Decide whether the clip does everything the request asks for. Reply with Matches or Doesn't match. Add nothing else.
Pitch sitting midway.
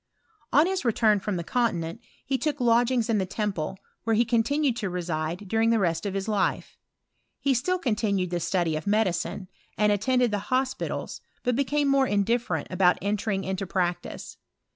Doesn't match